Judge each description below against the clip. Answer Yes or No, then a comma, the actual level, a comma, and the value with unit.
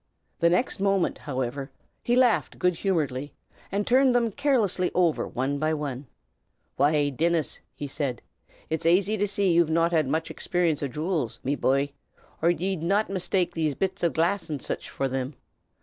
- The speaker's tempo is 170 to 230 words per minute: Yes, average, 175 wpm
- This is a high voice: No, medium, 165 Hz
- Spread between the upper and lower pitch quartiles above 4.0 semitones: Yes, average, 5.0 semitones